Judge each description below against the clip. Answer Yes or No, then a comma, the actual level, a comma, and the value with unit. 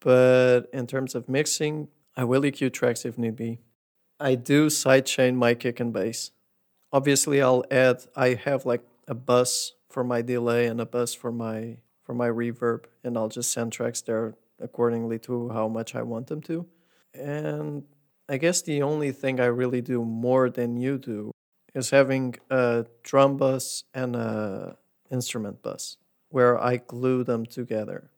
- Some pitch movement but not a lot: No, narrow, 2.2 semitones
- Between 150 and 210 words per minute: Yes, average, 170 wpm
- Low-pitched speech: Yes, low, 125 Hz